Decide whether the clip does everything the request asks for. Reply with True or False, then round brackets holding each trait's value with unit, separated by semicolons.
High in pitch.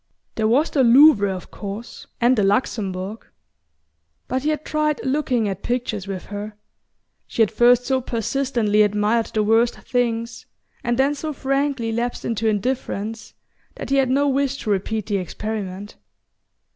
True (230 Hz)